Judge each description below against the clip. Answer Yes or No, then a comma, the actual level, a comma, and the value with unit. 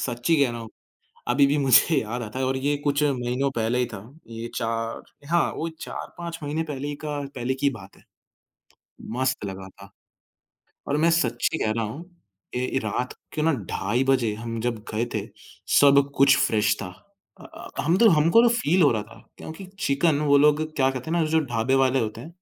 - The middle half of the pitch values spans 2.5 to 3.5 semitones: No, average, 4.2 semitones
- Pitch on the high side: No, low, 135 Hz